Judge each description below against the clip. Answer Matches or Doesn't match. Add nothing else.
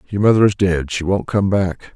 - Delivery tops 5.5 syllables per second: Doesn't match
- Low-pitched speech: Matches